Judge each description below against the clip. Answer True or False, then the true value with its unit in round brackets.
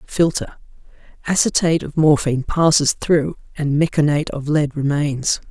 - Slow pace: True (120 wpm)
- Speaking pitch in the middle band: True (150 Hz)